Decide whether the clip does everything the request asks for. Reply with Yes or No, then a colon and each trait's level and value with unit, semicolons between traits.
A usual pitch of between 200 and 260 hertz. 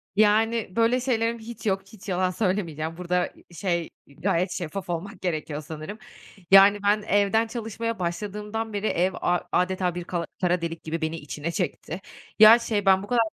No: high, 190 Hz